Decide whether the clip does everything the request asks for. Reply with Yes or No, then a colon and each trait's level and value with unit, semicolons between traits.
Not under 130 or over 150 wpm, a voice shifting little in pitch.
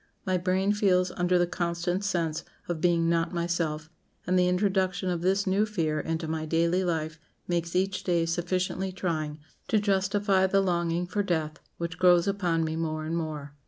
No: average, 175 wpm; narrow, 2.2 semitones